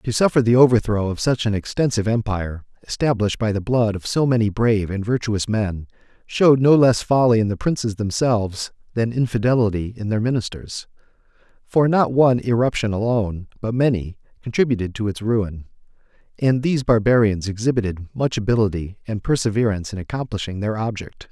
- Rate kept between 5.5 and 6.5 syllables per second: Yes, 5.8 syllables/s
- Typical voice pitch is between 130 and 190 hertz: No, low, 110 Hz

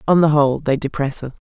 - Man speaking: No, female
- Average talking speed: No, fast, 245 wpm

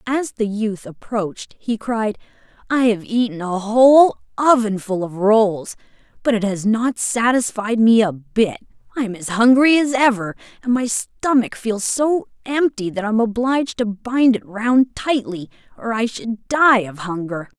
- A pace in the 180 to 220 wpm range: No, average, 165 wpm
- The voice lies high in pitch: Yes, high, 225 Hz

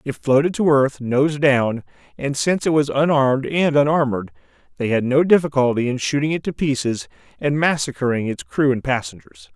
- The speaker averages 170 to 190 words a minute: Yes, average, 175 wpm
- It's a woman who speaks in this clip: No, male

